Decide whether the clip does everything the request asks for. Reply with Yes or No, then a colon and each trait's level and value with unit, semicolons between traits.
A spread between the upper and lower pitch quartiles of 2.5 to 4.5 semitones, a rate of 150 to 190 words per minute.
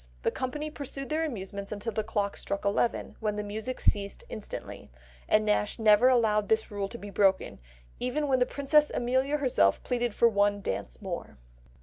Yes: average, 4.2 semitones; average, 180 wpm